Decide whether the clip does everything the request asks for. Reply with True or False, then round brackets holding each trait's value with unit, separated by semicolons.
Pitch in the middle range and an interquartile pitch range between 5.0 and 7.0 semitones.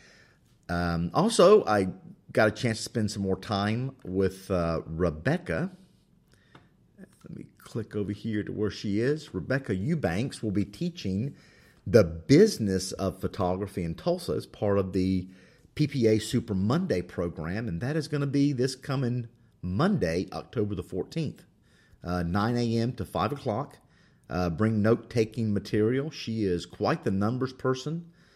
False (105 Hz; 5.5 semitones)